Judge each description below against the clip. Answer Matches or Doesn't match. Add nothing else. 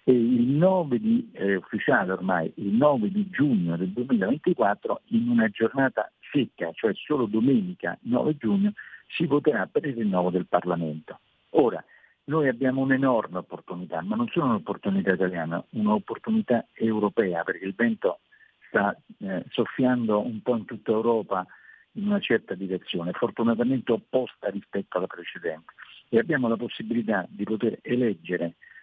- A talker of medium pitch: Doesn't match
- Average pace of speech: Matches